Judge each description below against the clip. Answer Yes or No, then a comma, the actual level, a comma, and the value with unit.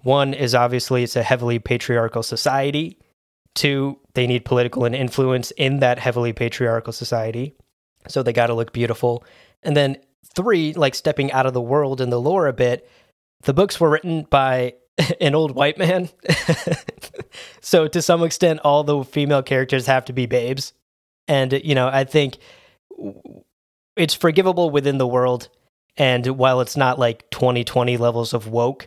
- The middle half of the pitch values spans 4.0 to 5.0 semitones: No, average, 3.0 semitones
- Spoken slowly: No, average, 165 wpm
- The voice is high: No, low, 130 Hz